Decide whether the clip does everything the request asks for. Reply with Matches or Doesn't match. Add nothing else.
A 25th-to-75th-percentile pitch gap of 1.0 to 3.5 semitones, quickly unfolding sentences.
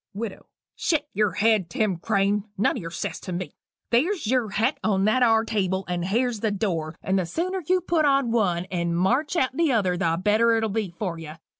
Doesn't match